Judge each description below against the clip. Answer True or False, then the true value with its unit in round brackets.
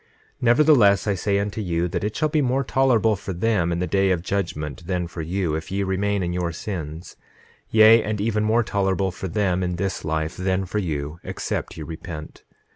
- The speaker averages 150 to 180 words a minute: False (205 wpm)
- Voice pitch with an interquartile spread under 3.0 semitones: False (3.7 semitones)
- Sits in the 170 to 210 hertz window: False (95 Hz)